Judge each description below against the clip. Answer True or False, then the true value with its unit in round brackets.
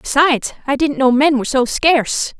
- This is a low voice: False (270 Hz)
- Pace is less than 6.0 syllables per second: True (5.5 syllables/s)